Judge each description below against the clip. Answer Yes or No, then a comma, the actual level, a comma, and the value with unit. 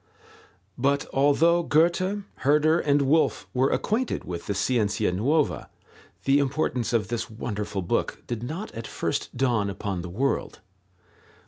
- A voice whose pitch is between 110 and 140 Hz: Yes, low, 135 Hz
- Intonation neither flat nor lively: No, wide, 6.4 semitones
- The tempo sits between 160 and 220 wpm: No, slow, 135 wpm